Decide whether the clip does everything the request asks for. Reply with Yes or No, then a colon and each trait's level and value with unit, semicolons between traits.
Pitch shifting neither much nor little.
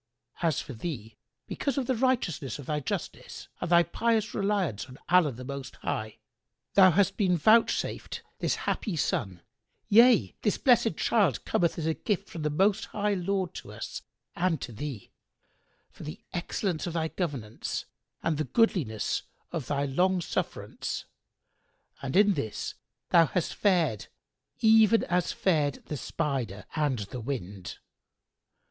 No: wide, 6.5 semitones